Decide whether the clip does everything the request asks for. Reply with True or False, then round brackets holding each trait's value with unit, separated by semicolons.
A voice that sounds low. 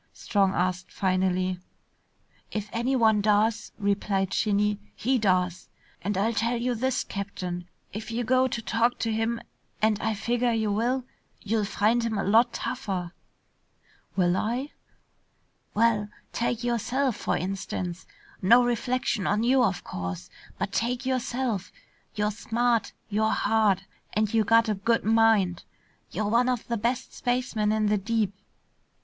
False (220 Hz)